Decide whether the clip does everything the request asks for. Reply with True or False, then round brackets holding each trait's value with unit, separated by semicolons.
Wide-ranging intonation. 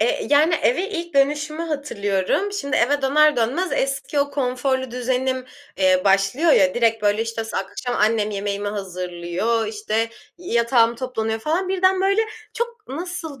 True (6.0 semitones)